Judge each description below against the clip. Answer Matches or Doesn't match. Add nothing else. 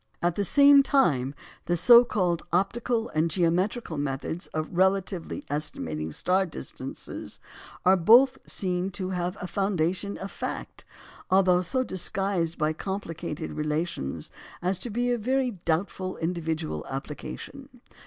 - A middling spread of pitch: Matches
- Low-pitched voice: Doesn't match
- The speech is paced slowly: Matches